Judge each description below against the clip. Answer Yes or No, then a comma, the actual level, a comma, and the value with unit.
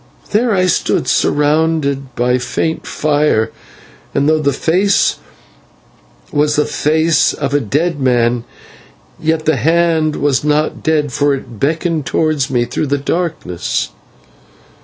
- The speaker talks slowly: Yes, slow, 130 wpm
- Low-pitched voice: No, medium, 150 Hz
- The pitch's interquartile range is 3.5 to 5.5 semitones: No, average, 2.7 semitones